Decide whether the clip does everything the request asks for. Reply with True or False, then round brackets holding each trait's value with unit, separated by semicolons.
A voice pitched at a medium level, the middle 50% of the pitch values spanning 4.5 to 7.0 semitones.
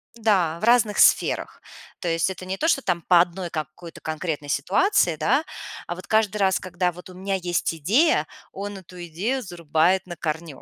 False (180 Hz; 3.4 semitones)